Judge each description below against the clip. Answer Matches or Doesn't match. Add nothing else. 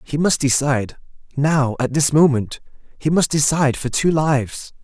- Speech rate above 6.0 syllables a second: Doesn't match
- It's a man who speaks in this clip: Matches